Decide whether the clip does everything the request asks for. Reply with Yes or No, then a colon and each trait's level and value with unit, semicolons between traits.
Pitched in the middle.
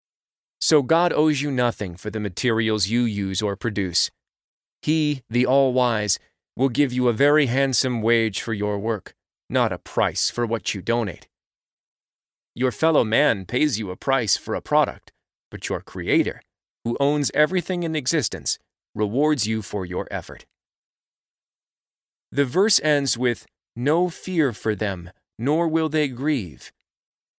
No: low, 125 Hz